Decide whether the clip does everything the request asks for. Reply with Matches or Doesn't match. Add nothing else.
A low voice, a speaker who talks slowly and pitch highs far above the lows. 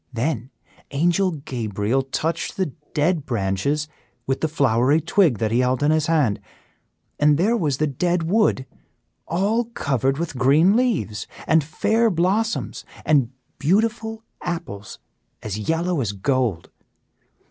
Doesn't match